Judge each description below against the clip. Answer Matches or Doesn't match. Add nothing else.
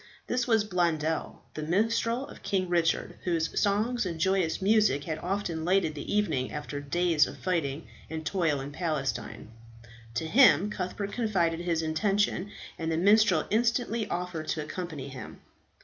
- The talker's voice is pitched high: Doesn't match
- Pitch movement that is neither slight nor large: Matches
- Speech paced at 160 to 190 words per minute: Doesn't match